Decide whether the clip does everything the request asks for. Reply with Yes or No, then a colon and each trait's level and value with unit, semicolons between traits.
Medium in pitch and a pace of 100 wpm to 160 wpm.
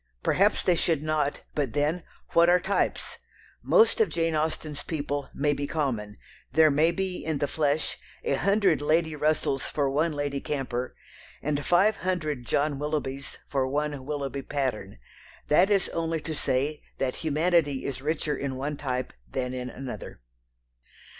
Yes: medium, 150 Hz; average, 155 wpm